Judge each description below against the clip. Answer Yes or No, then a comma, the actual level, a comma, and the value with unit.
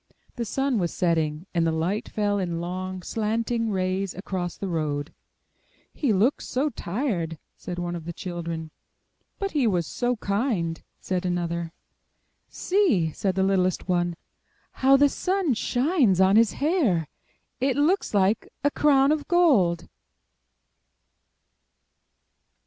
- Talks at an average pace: No, slow, 130 wpm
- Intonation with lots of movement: Yes, wide, 6.9 semitones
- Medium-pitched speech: No, high, 195 Hz